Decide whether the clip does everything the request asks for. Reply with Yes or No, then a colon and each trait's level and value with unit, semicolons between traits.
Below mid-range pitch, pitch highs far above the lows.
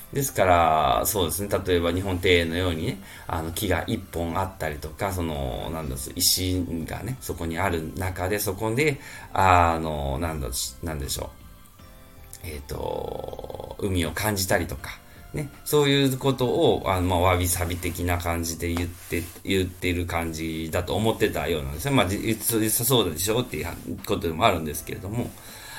No: very low, 90 Hz; average, 4.0 semitones